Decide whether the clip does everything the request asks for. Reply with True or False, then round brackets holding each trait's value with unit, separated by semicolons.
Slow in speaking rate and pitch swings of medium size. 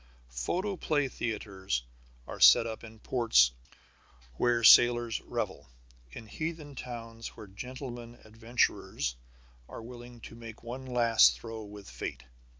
False (120 wpm; 2.1 semitones)